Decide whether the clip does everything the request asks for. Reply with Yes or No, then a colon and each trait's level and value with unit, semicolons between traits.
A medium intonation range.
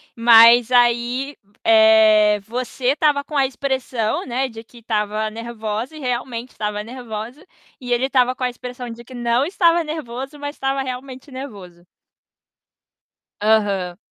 Yes: average, 3.2 semitones